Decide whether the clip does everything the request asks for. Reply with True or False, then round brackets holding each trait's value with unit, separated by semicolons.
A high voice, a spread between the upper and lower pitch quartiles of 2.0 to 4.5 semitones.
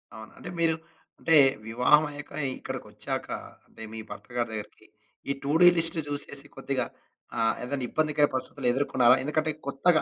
False (140 Hz; 3.5 semitones)